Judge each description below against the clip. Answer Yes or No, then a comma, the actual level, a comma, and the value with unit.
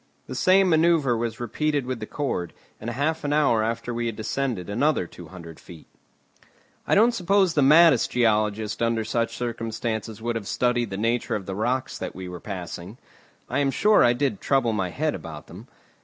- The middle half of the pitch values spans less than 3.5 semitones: No, average, 4.8 semitones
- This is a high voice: No, low, 120 Hz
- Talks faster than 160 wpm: Yes, average, 190 wpm